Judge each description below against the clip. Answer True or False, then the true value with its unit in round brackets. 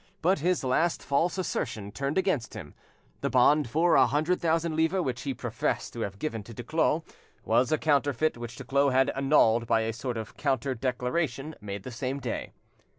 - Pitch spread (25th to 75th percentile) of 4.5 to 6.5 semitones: True (4.8 semitones)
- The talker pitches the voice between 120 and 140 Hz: True (135 Hz)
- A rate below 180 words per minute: False (185 wpm)